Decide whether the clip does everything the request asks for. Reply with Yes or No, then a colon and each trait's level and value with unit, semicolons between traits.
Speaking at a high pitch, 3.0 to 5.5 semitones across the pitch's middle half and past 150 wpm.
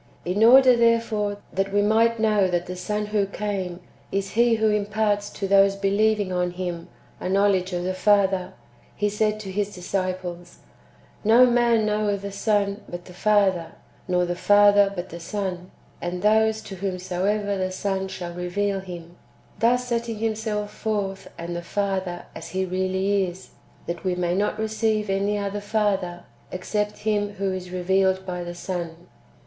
No: high, 195 Hz; narrow, 2.4 semitones; average, 170 wpm